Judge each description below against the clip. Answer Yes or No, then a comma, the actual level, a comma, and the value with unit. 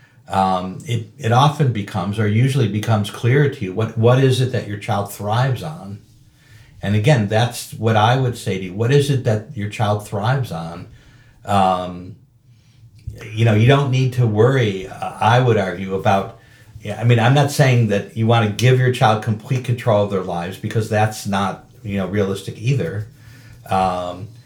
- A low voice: Yes, low, 115 Hz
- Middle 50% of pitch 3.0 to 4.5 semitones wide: Yes, average, 3.4 semitones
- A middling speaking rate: Yes, average, 185 wpm